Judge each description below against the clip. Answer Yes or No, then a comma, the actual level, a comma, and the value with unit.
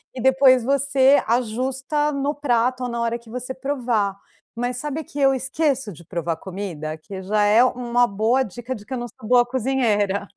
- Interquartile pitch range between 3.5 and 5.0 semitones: Yes, average, 4.0 semitones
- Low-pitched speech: No, high, 245 Hz